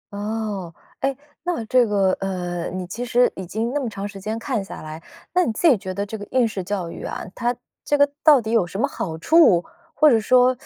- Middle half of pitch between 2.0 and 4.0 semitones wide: No, average, 4.8 semitones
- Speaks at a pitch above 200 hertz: Yes, high, 215 Hz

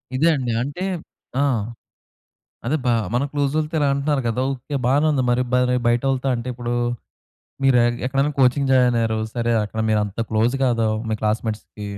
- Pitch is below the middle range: Yes, low, 125 Hz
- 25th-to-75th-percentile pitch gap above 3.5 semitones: No, average, 2.8 semitones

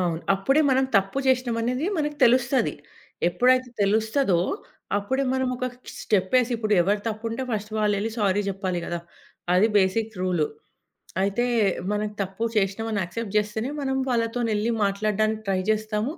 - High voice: Yes, high, 215 Hz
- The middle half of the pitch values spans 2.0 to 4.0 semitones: Yes, average, 3.7 semitones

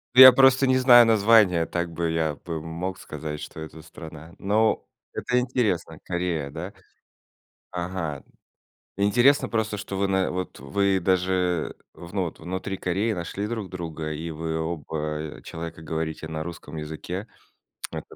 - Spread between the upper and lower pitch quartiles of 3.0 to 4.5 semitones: Yes, average, 4.0 semitones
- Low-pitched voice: Yes, very low, 90 Hz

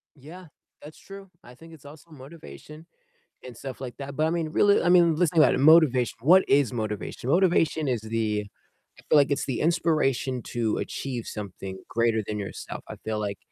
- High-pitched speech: No, medium, 140 Hz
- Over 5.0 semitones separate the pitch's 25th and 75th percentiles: Yes, wide, 5.6 semitones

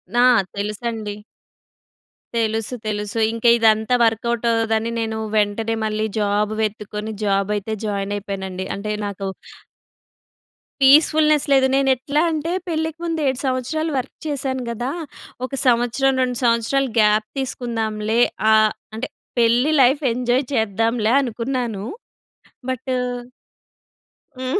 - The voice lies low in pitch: No, high, 230 Hz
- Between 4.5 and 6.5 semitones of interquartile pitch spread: No, average, 3.4 semitones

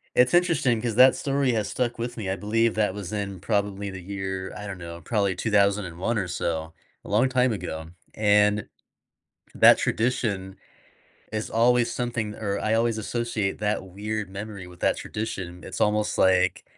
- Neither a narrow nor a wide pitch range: Yes, average, 3.3 semitones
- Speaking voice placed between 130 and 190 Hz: No, low, 105 Hz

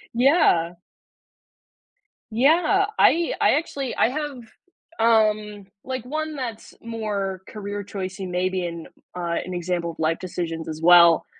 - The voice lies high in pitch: Yes, high, 205 Hz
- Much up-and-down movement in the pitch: Yes, wide, 6.6 semitones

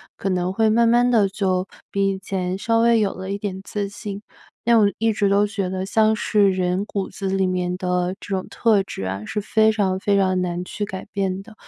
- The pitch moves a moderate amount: No, narrow, 2.2 semitones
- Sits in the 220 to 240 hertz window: No, high, 195 Hz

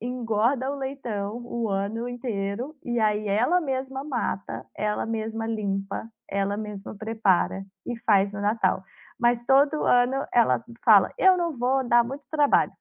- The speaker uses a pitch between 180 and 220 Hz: No, high, 230 Hz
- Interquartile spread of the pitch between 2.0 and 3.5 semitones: No, average, 3.9 semitones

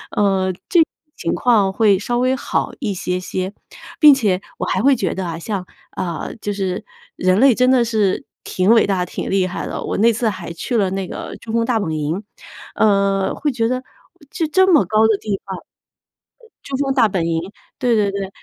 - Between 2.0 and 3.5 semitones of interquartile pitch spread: No, average, 4.3 semitones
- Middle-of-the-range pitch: No, high, 205 Hz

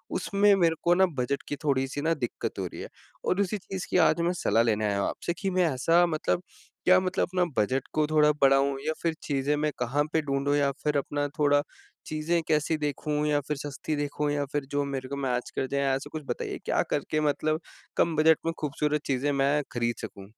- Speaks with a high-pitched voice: No, medium, 145 Hz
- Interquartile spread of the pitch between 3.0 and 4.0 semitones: No, narrow, 2.6 semitones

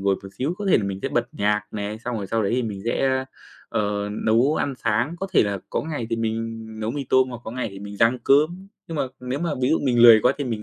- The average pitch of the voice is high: No, low, 115 Hz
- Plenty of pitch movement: No, average, 4.1 semitones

